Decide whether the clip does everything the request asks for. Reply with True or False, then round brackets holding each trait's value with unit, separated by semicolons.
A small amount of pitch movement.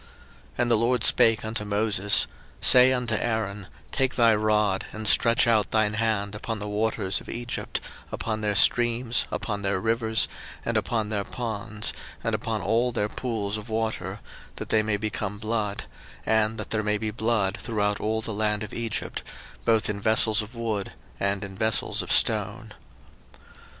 True (1.7 semitones)